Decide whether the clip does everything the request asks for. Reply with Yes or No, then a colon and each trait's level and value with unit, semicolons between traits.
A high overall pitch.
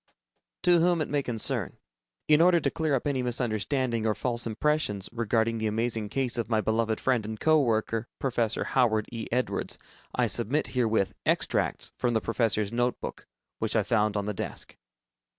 No: low, 115 Hz